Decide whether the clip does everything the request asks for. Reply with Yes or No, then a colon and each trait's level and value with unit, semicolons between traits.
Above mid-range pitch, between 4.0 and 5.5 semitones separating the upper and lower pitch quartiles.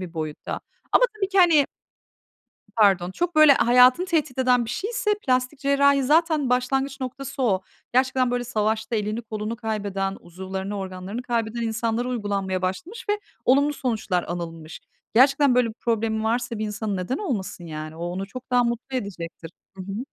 Yes: high, 235 Hz; average, 5.2 semitones